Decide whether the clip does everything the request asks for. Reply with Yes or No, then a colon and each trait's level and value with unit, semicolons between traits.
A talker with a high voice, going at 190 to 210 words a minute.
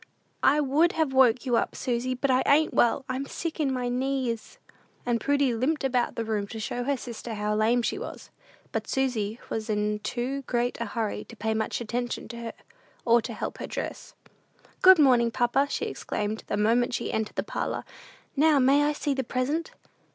Yes: high, 245 Hz; average, 195 wpm